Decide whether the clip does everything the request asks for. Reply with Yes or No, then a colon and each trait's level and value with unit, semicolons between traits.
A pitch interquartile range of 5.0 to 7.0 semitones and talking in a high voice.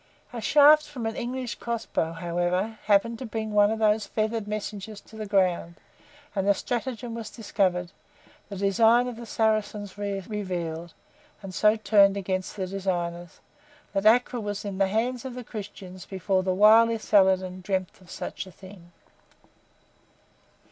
No: average, 3.0 semitones; high, 205 Hz